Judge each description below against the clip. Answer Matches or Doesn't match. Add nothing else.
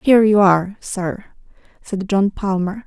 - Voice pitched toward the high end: Matches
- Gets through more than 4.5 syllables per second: Doesn't match